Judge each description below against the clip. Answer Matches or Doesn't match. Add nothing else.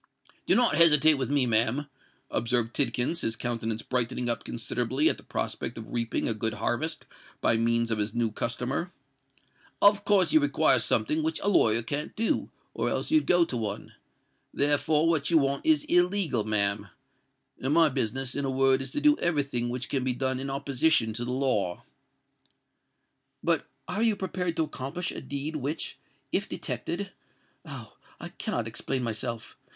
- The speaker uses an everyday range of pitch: Doesn't match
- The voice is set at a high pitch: Doesn't match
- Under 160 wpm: Doesn't match